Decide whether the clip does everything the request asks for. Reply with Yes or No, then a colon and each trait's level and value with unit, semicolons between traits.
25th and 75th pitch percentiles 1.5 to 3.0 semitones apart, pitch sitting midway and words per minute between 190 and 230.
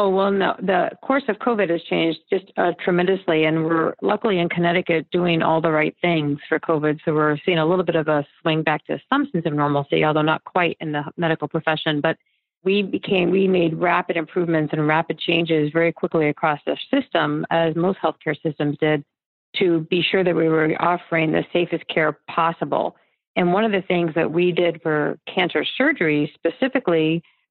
Yes: narrow, 2.4 semitones; medium, 165 Hz; average, 195 wpm